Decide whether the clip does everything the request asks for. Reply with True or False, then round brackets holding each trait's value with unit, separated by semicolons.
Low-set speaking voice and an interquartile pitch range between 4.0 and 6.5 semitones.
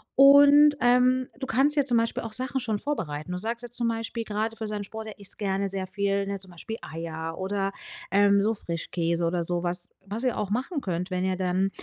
False (205 Hz; 4.7 semitones)